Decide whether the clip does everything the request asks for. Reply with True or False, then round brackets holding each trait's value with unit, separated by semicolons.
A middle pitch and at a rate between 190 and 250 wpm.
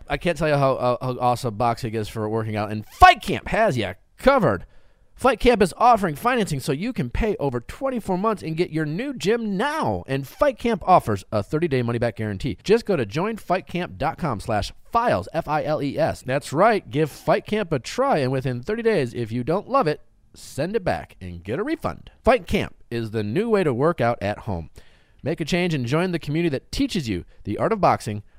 True (150 Hz; 205 wpm)